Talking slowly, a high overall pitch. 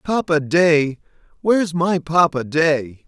No: slow, 115 wpm; medium, 160 Hz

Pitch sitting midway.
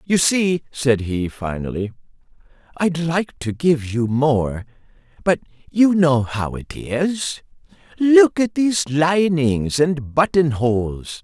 Yes: medium, 150 Hz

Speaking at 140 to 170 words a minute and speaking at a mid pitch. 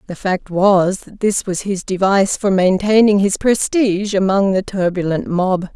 No: average, 165 wpm; high, 195 Hz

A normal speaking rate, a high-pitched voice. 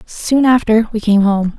Yes: average, 190 wpm; high, 220 Hz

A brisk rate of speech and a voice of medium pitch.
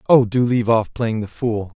No: fast, 235 wpm; low, 115 Hz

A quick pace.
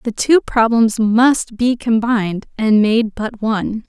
No: average, 155 wpm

